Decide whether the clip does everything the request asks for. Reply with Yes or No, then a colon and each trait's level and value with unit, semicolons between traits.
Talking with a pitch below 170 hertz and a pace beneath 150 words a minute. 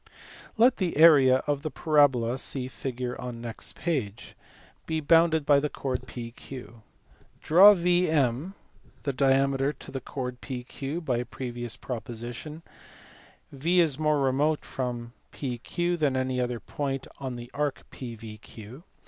Yes: low, 135 Hz; average, 140 wpm